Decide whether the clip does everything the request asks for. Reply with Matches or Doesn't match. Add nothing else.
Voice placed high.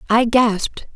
Matches